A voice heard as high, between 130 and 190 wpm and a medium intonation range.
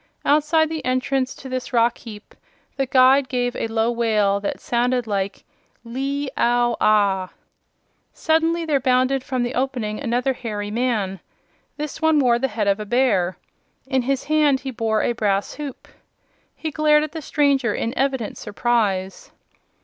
Yes: very high, 250 Hz; average, 155 wpm; average, 3.9 semitones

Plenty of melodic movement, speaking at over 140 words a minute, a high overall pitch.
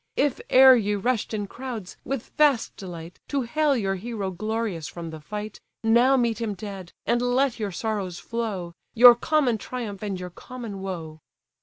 No: average, 4.3 semitones; average, 170 wpm; high, 220 Hz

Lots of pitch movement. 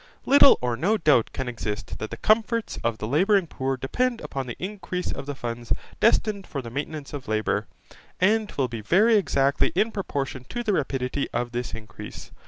Yes: wide, 9.0 semitones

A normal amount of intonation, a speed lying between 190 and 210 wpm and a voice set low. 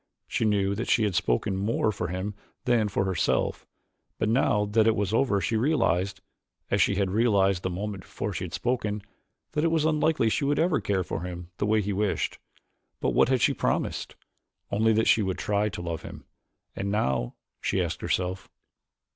Yes: average, 3.0 semitones; average, 195 wpm; low, 105 Hz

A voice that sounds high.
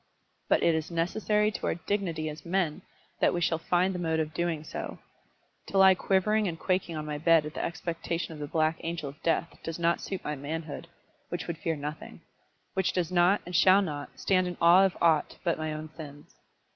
No: medium, 170 Hz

